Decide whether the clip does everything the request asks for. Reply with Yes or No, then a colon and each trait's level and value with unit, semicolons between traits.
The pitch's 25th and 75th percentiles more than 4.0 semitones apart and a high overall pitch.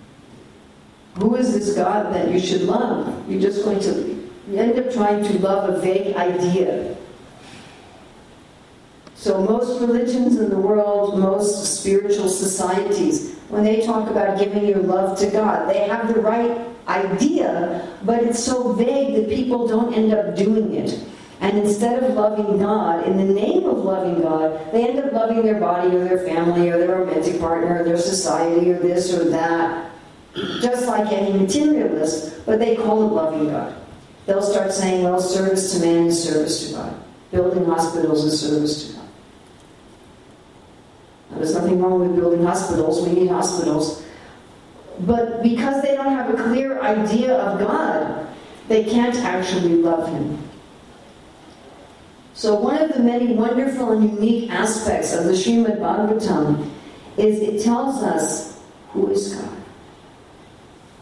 Yes: average, 4.5 semitones; high, 200 Hz